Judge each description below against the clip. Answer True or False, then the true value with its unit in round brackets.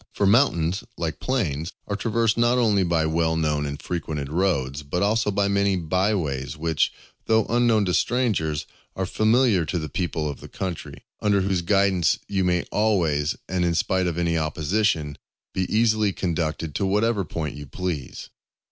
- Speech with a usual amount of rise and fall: True (4.6 semitones)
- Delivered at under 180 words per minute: True (170 wpm)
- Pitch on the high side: False (90 Hz)